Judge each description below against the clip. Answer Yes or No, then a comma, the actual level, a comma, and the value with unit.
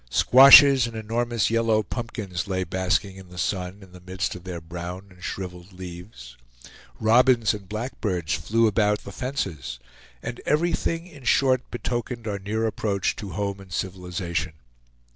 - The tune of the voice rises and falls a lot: No, average, 4.2 semitones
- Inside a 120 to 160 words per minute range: Yes, average, 150 wpm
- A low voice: Yes, low, 100 Hz